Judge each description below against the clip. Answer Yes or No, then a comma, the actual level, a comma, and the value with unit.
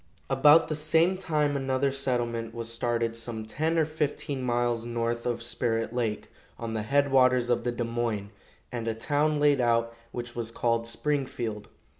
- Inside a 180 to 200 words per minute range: No, average, 170 wpm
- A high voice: No, low, 120 Hz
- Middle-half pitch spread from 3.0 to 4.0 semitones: Yes, average, 3.5 semitones